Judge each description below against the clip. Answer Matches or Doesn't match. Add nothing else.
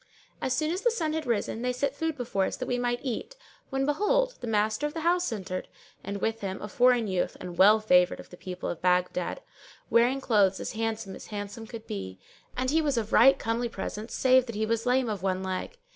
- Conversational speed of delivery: Doesn't match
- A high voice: Matches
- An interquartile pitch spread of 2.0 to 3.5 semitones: Doesn't match